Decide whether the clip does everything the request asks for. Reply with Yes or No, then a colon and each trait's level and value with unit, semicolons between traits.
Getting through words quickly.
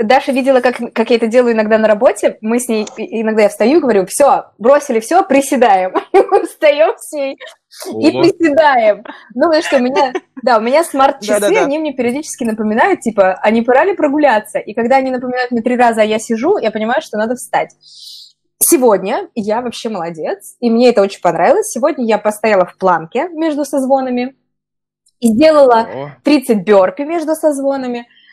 Yes: fast, 165 wpm